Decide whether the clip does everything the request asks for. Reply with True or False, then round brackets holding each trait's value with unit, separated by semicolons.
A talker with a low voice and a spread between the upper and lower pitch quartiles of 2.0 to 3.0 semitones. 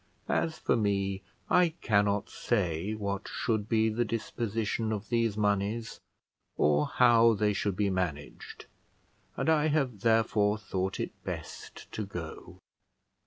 True (105 Hz; 2.6 semitones)